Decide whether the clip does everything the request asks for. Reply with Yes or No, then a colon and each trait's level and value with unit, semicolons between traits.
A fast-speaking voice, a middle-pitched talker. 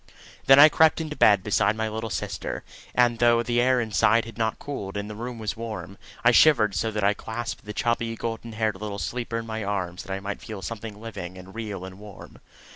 No: fast, 220 wpm; low, 110 Hz